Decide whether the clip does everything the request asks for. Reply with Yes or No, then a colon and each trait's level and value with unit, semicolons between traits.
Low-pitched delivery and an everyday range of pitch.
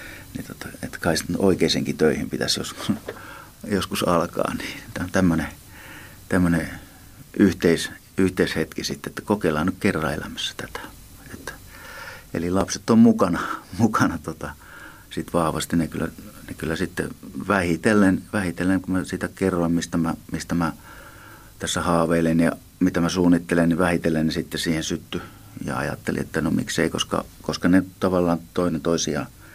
No: very low, 90 Hz; narrow, 2.2 semitones